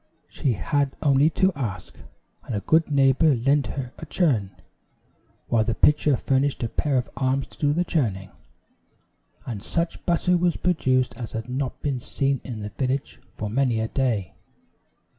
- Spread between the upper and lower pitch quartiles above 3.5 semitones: Yes, average, 4.1 semitones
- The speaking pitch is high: No, low, 135 Hz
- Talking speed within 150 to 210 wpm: Yes, average, 165 wpm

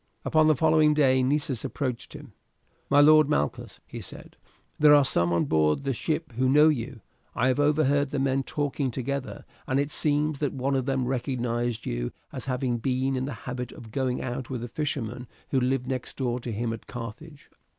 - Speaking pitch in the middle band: No, low, 130 Hz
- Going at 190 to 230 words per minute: Yes, average, 195 wpm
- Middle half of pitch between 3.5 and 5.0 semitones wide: No, average, 2.9 semitones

